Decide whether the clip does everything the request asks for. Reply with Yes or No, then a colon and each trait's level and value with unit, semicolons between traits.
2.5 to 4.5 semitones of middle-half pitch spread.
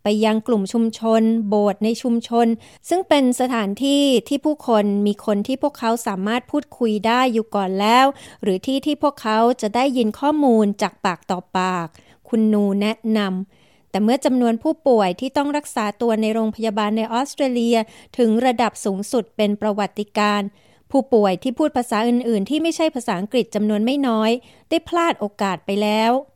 Yes: average, 3.5 semitones